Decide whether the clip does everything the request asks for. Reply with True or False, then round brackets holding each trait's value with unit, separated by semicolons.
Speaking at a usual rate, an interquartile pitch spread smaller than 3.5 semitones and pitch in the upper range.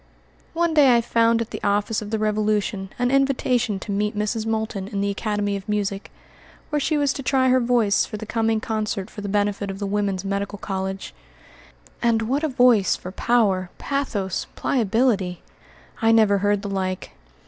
True (180 wpm; 2.9 semitones; 215 Hz)